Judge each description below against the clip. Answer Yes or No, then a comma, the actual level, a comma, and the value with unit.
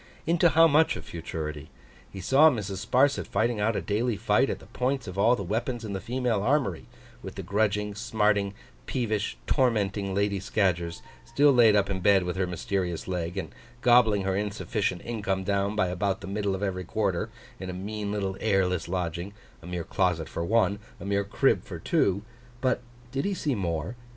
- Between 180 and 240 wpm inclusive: Yes, average, 190 wpm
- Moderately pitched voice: No, low, 100 Hz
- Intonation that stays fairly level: No, average, 3.4 semitones